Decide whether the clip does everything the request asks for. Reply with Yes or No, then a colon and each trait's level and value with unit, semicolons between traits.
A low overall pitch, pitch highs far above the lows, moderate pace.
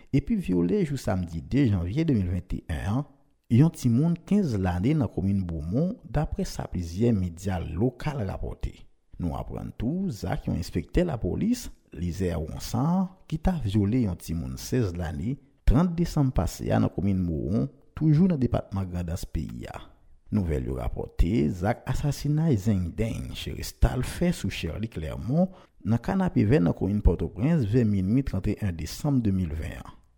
Yes: low, 110 Hz; wide, 8.3 semitones; average, 160 wpm